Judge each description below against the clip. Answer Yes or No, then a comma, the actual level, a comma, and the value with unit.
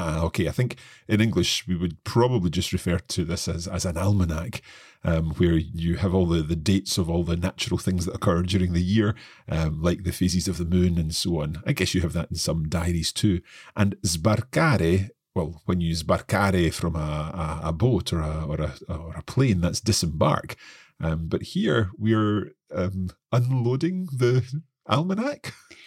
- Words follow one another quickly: No, average, 190 wpm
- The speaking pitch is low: Yes, very low, 90 Hz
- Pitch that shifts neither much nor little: Yes, average, 3.9 semitones